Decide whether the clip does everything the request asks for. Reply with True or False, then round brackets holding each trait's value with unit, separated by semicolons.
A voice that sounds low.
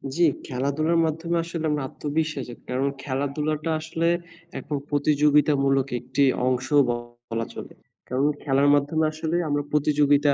False (145 Hz)